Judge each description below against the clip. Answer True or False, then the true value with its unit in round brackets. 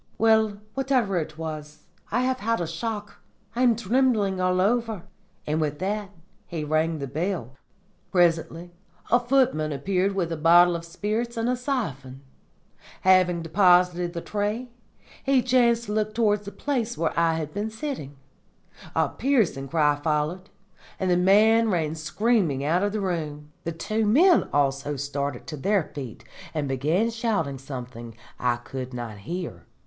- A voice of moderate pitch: True (180 Hz)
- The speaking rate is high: False (155 wpm)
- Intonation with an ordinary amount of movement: False (6.4 semitones)